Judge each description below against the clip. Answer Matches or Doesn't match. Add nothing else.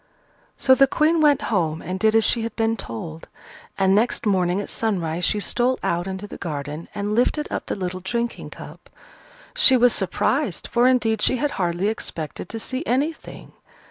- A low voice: Doesn't match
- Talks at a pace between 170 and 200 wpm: Matches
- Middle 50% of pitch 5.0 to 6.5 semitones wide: Matches